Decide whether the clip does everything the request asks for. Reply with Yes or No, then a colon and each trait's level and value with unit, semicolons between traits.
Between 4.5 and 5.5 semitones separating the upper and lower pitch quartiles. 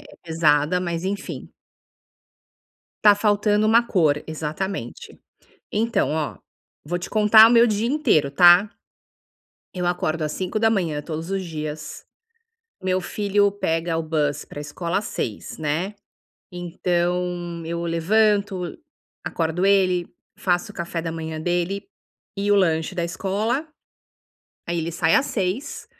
No: average, 3.8 semitones